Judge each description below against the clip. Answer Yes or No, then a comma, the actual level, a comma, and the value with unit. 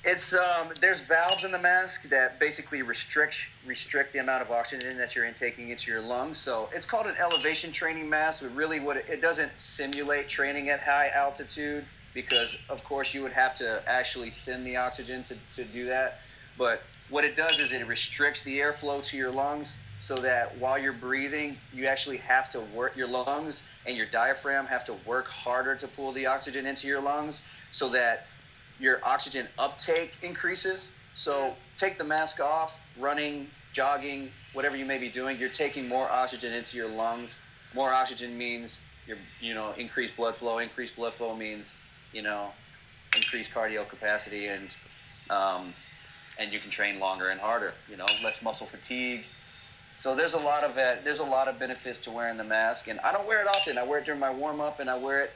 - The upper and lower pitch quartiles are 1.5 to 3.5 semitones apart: Yes, average, 3.1 semitones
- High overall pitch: No, low, 135 Hz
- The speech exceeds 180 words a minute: Yes, average, 195 wpm